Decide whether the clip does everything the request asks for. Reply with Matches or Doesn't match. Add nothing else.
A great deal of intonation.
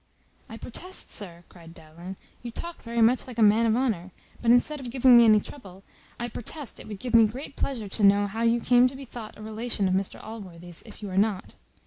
Doesn't match